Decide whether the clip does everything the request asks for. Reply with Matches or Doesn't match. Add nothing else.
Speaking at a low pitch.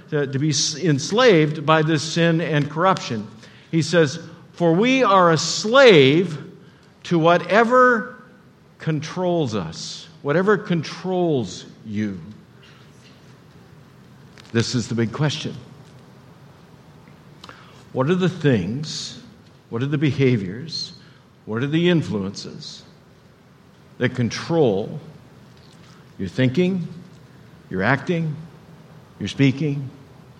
Doesn't match